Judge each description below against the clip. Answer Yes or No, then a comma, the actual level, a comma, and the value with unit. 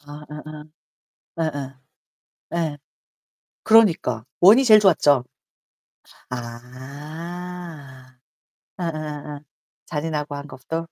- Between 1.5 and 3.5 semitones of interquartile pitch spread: Yes, average, 3.1 semitones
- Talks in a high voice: No, medium, 150 Hz